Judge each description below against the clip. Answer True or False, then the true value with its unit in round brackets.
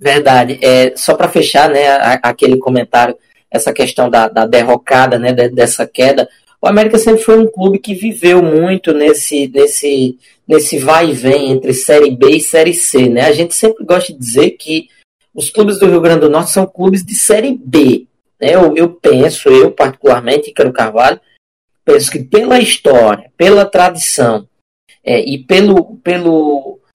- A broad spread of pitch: True (6.6 semitones)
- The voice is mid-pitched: True (165 Hz)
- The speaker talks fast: False (165 wpm)